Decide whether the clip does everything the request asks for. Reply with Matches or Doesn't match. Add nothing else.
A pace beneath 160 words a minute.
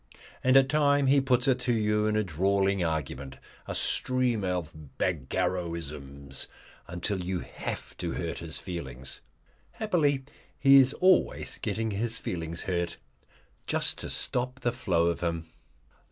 Matches